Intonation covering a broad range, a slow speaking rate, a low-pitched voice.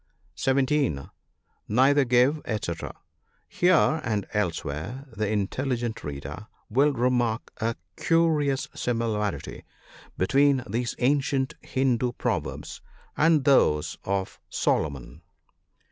No: average, 4.8 semitones; slow, 100 wpm; low, 120 Hz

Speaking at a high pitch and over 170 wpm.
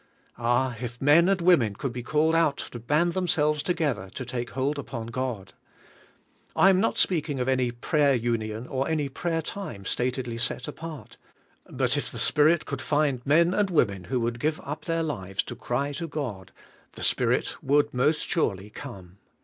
No: low, 135 Hz; average, 180 wpm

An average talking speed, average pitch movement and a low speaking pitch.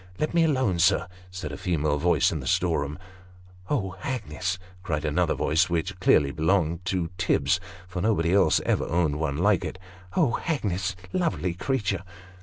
Yes: average, 180 wpm; average, 3.4 semitones; very low, 90 Hz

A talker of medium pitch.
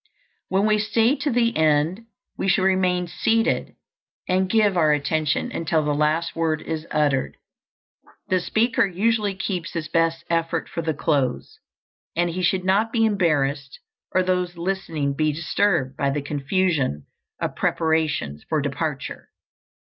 Yes: medium, 165 Hz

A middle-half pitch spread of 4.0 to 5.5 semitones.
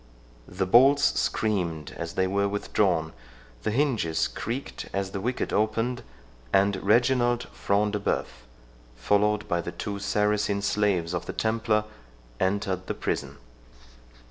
No: average, 2.8 semitones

